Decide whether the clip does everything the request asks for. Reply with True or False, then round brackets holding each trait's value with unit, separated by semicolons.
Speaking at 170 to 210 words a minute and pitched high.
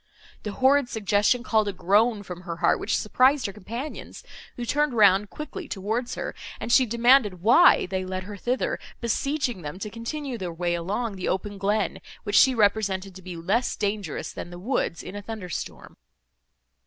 True (180 wpm; 210 Hz)